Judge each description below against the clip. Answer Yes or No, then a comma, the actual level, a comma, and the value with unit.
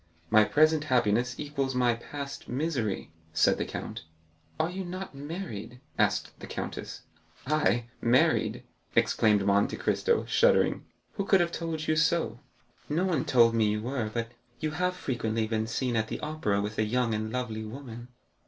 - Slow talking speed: No, average, 160 wpm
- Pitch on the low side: Yes, low, 125 Hz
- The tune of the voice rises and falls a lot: Yes, wide, 5.9 semitones